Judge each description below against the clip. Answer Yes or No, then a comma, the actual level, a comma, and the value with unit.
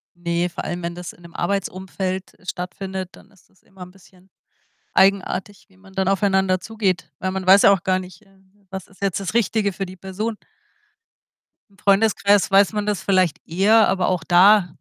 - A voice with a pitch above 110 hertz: Yes, high, 190 Hz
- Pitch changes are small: Yes, narrow, 1.5 semitones